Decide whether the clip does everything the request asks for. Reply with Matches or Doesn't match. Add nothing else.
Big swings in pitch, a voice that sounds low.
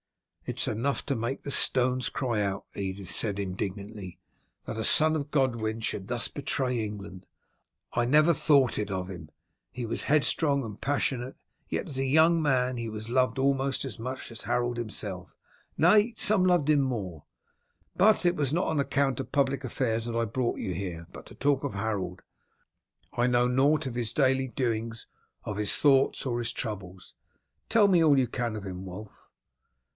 Doesn't match